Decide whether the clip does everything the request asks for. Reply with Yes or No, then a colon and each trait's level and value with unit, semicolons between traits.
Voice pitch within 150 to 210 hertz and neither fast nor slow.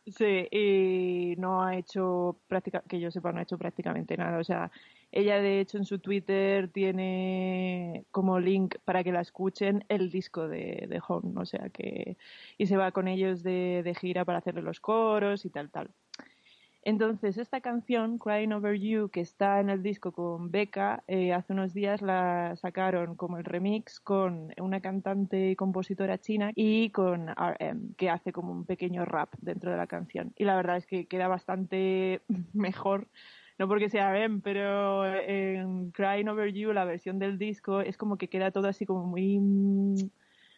Yes: high, 190 Hz; average, 180 wpm